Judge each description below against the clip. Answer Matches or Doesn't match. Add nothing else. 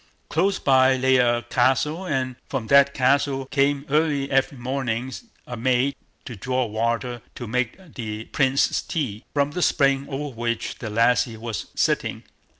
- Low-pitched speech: Matches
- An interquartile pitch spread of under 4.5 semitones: Matches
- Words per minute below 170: Matches